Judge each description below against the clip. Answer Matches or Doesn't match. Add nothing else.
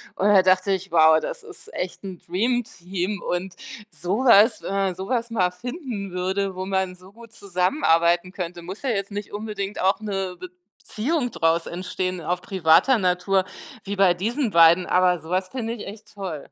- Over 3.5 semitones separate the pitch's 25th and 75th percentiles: Doesn't match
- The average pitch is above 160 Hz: Matches